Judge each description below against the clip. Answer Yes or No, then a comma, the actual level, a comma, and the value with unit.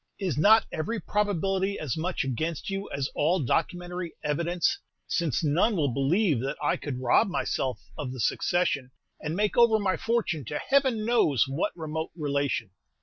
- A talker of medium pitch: Yes, medium, 170 Hz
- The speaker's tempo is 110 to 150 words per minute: No, average, 165 wpm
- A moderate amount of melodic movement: No, wide, 5.7 semitones